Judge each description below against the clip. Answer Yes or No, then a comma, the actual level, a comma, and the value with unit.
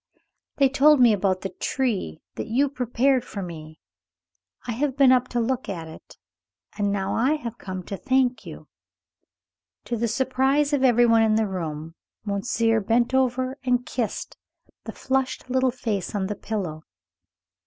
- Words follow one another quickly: No, average, 165 wpm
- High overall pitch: Yes, high, 235 Hz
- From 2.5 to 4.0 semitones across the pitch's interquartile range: No, average, 4.6 semitones